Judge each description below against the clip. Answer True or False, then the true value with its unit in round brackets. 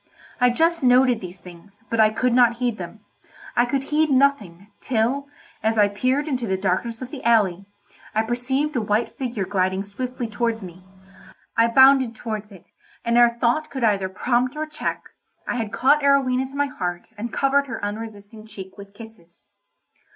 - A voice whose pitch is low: False (230 Hz)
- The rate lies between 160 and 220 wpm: True (180 wpm)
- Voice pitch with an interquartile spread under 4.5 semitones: True (4.1 semitones)